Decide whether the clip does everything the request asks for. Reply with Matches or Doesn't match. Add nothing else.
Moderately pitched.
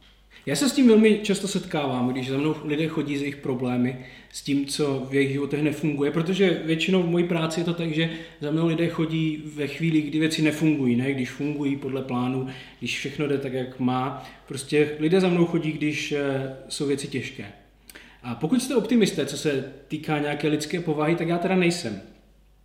Matches